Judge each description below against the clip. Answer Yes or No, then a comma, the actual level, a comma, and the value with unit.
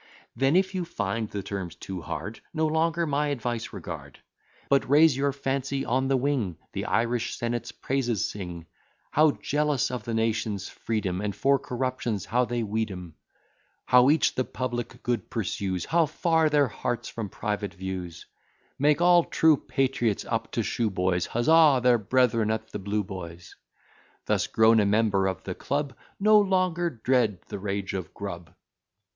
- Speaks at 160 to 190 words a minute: Yes, average, 165 wpm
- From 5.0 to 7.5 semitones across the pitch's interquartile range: Yes, wide, 5.4 semitones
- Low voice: Yes, low, 120 Hz